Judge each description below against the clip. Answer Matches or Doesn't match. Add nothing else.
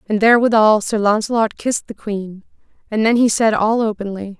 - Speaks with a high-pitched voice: Matches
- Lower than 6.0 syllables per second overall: Matches